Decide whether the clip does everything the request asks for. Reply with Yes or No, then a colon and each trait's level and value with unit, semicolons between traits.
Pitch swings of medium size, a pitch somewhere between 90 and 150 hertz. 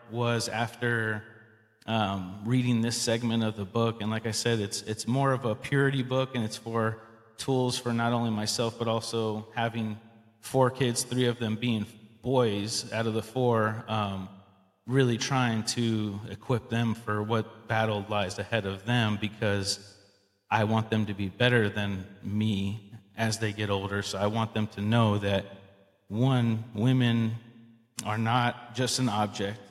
No: narrow, 2.0 semitones; low, 110 Hz